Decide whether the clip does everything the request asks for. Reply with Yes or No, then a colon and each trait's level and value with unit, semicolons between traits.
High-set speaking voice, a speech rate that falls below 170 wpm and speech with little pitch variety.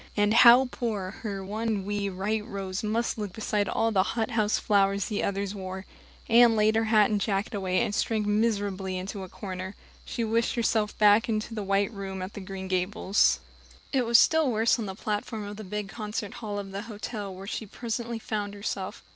No: high, 210 Hz; average, 195 wpm; narrow, 2.2 semitones